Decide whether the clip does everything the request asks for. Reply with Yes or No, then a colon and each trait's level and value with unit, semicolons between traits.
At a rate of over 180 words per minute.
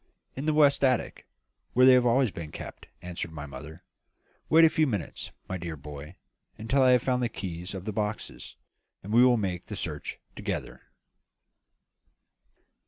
No: average, 170 wpm